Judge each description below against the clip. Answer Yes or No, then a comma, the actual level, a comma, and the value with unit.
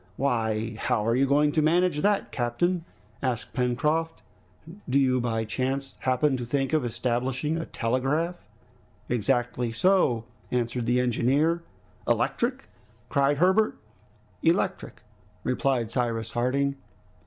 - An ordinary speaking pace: No, slow, 120 wpm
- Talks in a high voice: No, low, 130 Hz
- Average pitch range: Yes, average, 3.9 semitones